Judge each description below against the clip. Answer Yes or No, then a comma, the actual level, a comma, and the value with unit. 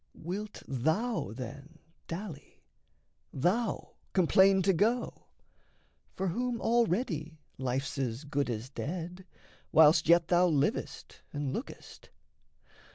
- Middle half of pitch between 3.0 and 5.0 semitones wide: No, wide, 5.6 semitones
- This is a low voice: No, medium, 170 Hz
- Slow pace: Yes, slow, 100 wpm